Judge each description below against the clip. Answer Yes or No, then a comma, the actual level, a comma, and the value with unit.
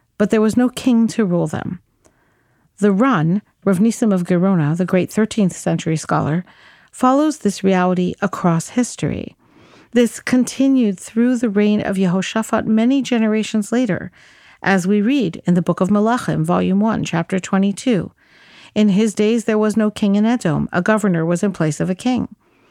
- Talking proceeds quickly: No, average, 165 wpm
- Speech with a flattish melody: No, average, 3.7 semitones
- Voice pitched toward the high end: Yes, high, 210 Hz